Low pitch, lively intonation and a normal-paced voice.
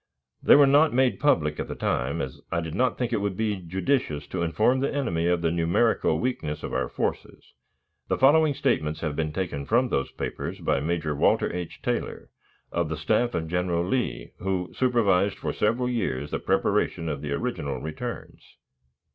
Yes: very low, 90 Hz; wide, 7.6 semitones; average, 185 wpm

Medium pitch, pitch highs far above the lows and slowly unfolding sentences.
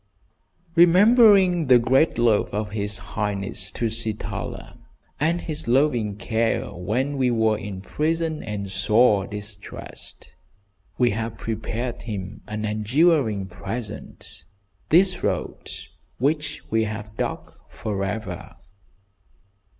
No: low, 115 Hz; wide, 6.1 semitones; slow, 110 wpm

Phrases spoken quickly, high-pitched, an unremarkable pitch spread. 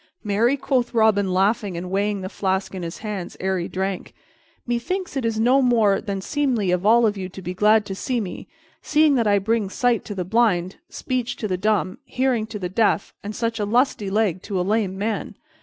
Yes: fast, 210 wpm; high, 210 Hz; average, 3.7 semitones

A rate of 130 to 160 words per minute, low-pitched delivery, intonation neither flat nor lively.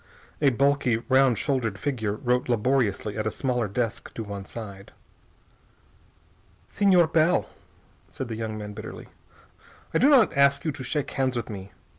Yes: average, 155 wpm; low, 125 Hz; average, 4.4 semitones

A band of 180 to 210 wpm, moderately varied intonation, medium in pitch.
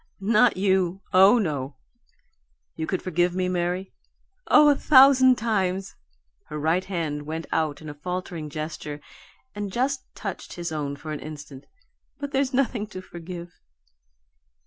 No: average, 145 wpm; average, 4.9 semitones; medium, 180 Hz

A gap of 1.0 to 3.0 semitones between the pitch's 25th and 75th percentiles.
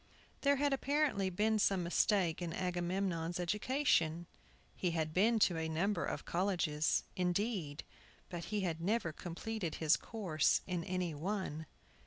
No: average, 3.9 semitones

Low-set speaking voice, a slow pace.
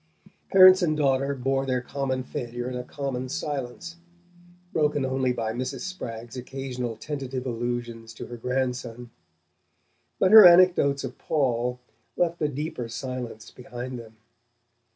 Yes: low, 130 Hz; slow, 130 wpm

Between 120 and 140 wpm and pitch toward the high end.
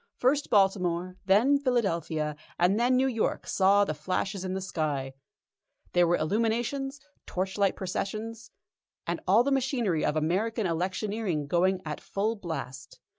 Yes: slow, 135 wpm; high, 195 Hz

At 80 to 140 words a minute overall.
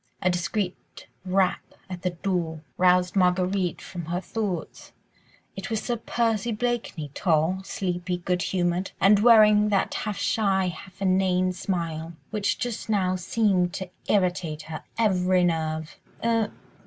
Yes: slow, 135 wpm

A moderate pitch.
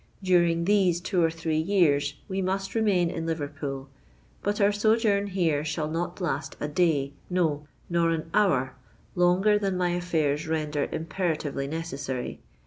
Yes: medium, 170 Hz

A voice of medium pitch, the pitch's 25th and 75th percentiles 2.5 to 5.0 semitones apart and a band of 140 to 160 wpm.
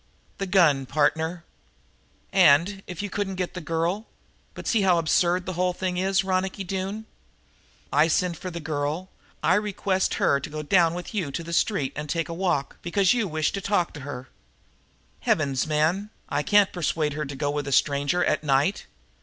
No: medium, 170 Hz; average, 4.0 semitones; average, 185 wpm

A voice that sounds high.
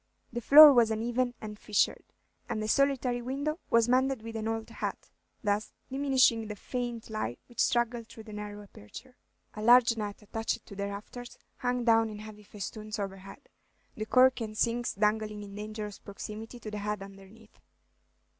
Yes: high, 220 Hz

